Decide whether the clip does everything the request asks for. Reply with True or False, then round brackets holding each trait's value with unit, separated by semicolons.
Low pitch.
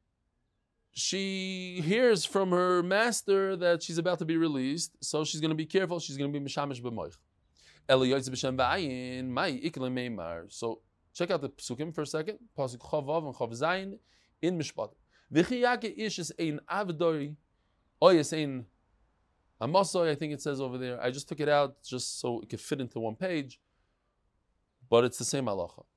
False (150 Hz)